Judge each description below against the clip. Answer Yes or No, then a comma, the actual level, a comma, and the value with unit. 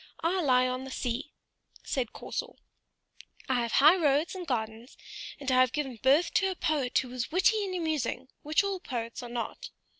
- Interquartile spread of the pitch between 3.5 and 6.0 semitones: Yes, average, 5.0 semitones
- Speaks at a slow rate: No, average, 185 wpm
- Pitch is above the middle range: Yes, very high, 270 Hz